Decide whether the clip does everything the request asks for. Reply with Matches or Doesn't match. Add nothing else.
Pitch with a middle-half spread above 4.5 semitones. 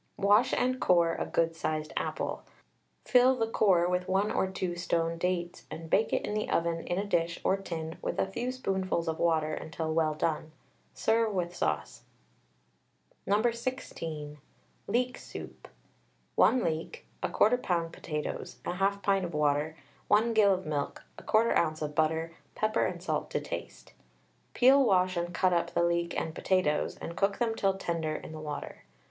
Doesn't match